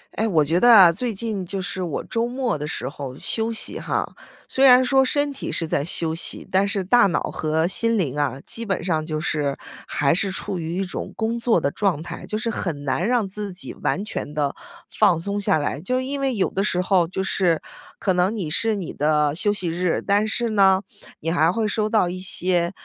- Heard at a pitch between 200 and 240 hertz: No, high, 190 Hz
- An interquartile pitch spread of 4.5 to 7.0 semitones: Yes, average, 5.2 semitones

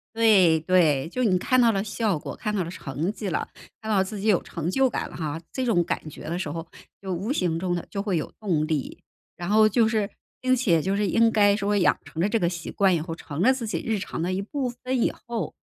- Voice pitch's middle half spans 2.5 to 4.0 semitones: No, average, 4.6 semitones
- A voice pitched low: No, high, 195 Hz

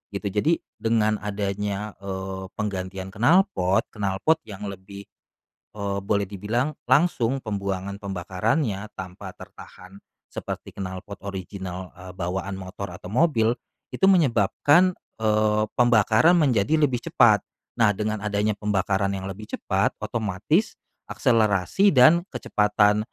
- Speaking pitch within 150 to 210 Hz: No, low, 105 Hz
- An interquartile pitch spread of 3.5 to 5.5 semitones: No, average, 3.1 semitones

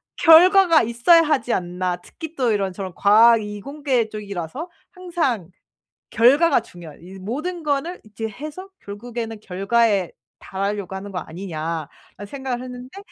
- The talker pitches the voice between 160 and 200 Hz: No, high, 230 Hz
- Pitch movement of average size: No, wide, 6.9 semitones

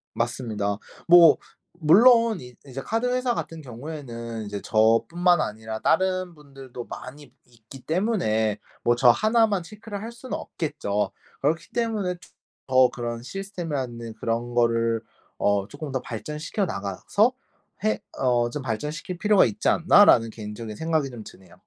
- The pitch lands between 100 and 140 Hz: Yes, low, 135 Hz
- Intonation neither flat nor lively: No, wide, 7.7 semitones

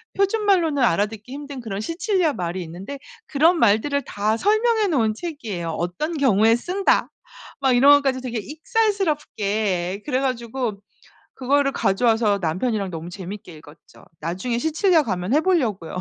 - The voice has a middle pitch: No, high, 245 Hz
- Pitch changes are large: Yes, wide, 7.4 semitones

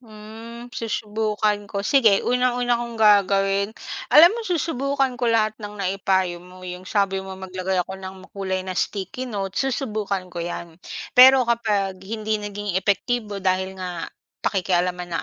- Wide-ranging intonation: No, average, 3.5 semitones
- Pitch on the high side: Yes, high, 205 Hz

